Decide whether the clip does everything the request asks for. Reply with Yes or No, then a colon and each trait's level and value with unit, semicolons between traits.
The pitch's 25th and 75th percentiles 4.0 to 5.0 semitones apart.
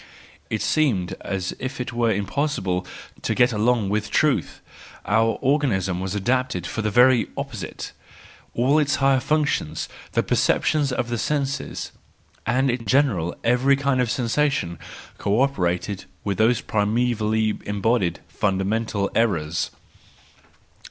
Yes: average, 4.7 semitones